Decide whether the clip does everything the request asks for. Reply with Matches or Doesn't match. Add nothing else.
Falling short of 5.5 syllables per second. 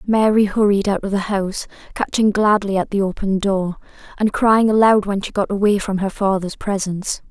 Matches